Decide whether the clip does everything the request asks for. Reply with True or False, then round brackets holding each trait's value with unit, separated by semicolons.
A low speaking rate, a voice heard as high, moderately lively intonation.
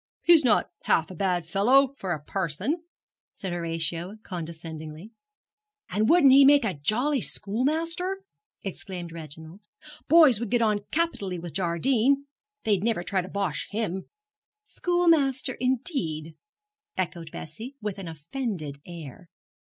False (130 wpm; 200 Hz; 7.9 semitones)